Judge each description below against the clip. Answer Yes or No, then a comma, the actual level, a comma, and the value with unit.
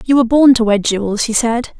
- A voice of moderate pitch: No, high, 235 Hz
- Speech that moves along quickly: Yes, fast, 265 wpm